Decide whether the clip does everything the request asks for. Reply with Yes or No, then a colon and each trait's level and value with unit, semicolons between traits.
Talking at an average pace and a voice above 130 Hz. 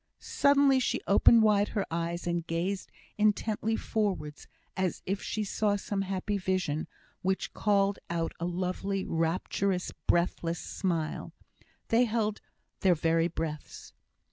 No: slow, 125 wpm; high, 190 Hz